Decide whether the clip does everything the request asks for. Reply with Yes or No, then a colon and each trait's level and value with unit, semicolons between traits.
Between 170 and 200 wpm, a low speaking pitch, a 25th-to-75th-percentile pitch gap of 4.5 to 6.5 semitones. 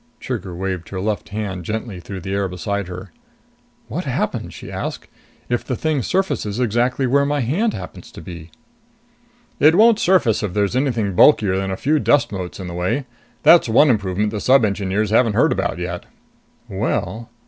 Yes: average, 180 wpm; low, 105 Hz; wide, 5.5 semitones